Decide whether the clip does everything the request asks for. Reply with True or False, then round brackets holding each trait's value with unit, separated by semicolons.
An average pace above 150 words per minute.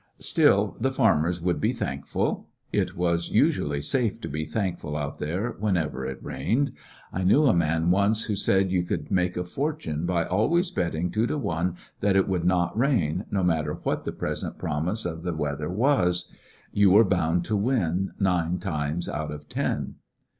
True (180 wpm)